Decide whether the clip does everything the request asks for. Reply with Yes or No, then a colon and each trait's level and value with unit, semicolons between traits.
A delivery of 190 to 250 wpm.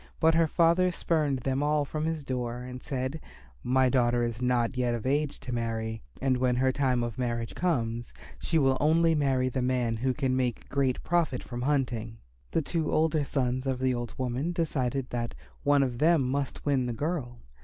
Yes: average, 195 wpm